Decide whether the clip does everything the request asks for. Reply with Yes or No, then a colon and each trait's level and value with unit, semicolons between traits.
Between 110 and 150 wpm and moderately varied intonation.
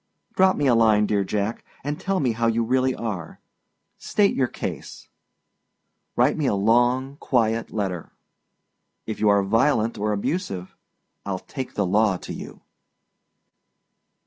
Yes: average, 145 wpm; average, 4.2 semitones